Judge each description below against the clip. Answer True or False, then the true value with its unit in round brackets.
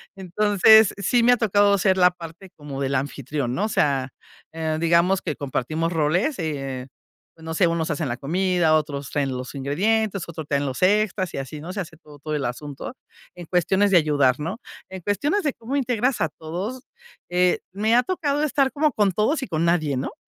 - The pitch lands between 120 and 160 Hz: False (170 Hz)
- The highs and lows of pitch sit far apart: True (5.9 semitones)